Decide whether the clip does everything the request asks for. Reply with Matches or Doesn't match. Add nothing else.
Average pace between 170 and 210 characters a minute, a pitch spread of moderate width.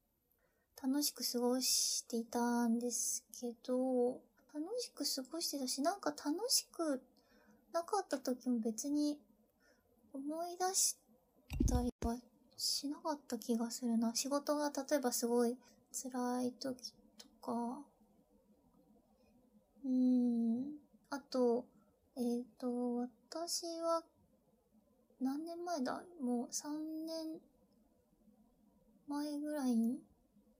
Matches